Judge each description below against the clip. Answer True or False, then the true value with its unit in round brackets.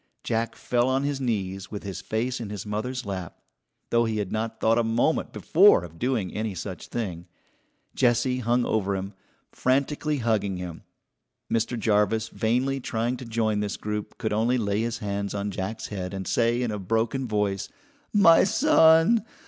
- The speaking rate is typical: True (175 wpm)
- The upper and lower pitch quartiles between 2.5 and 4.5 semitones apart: True (3.5 semitones)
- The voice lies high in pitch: False (110 Hz)